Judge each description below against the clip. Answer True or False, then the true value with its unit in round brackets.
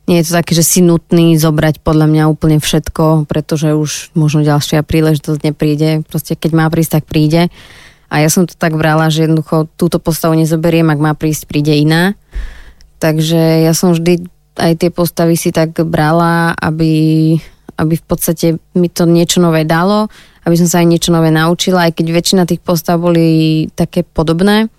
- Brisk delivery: True (180 wpm)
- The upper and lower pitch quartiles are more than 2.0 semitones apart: False (1.6 semitones)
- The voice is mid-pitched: True (165 Hz)